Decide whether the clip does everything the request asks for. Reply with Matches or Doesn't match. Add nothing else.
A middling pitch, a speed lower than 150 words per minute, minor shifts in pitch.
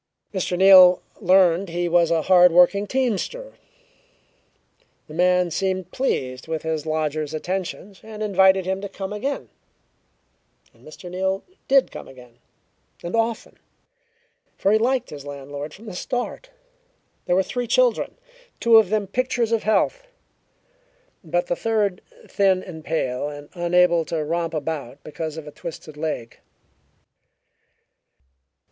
Doesn't match